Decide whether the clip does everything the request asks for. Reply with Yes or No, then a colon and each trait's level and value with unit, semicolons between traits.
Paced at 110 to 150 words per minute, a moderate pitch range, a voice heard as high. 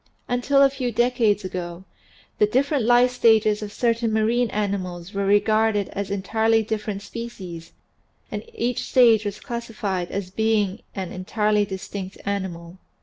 Yes: average, 145 wpm; average, 3.2 semitones; high, 210 Hz